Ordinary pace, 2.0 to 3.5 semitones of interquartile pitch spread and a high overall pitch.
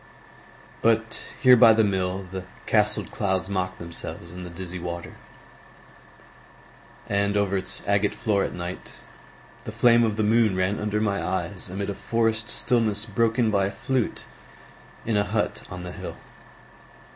No: average, 155 wpm; average, 3.0 semitones; low, 100 Hz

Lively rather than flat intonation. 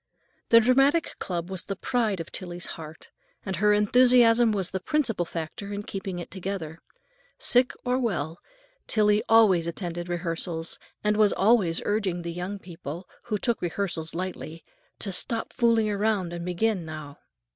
No: average, 4.2 semitones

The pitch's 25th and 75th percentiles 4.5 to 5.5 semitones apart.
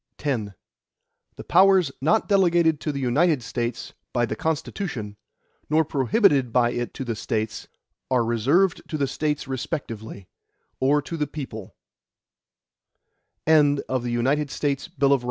Yes: average, 5.2 semitones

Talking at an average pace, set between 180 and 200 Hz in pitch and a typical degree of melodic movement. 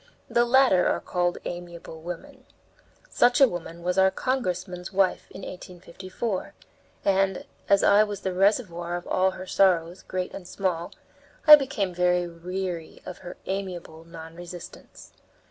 No: average, 145 wpm; medium, 185 Hz; narrow, 1.9 semitones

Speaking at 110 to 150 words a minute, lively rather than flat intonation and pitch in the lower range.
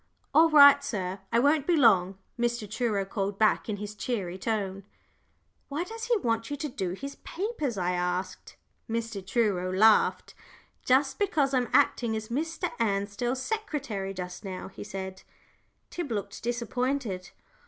No: average, 145 wpm; wide, 6.3 semitones; high, 225 Hz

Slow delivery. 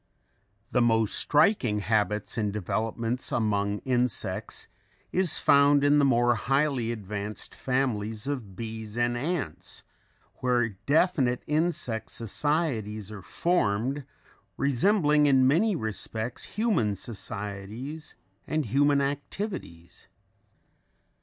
Yes: slow, 100 wpm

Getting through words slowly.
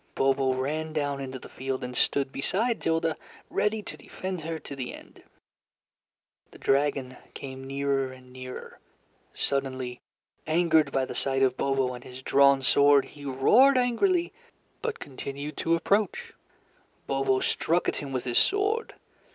No: average, 150 wpm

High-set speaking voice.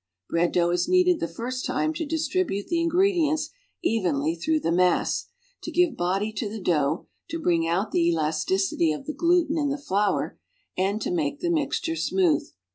Yes: high, 225 Hz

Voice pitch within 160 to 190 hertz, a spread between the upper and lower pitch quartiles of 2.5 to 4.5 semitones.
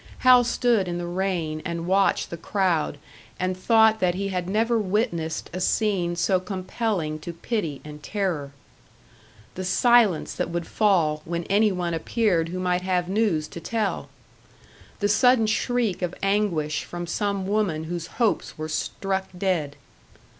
Yes: medium, 185 Hz; average, 3.7 semitones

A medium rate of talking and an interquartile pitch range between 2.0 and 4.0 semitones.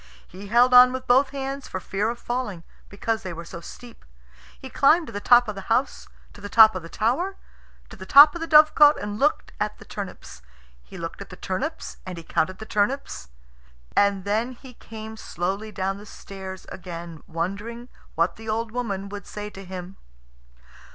No: average, 195 wpm; average, 4.5 semitones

